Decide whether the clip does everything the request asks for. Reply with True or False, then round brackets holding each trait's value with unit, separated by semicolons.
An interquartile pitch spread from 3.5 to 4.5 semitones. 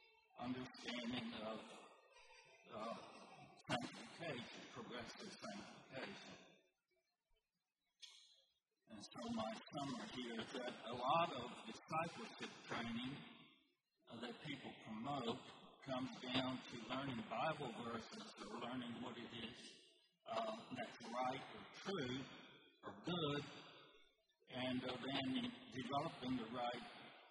False (3.0 semitones)